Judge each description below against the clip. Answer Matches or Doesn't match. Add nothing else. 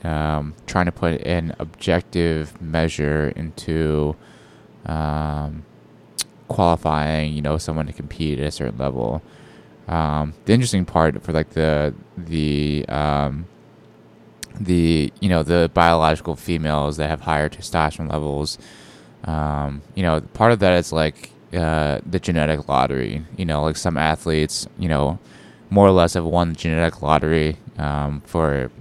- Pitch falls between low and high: Doesn't match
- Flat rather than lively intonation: Matches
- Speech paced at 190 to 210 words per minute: Doesn't match